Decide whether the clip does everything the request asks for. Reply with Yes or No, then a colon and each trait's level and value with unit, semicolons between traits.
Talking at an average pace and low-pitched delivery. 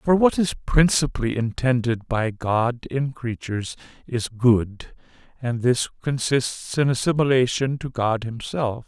No: slow, 130 wpm; low, 125 Hz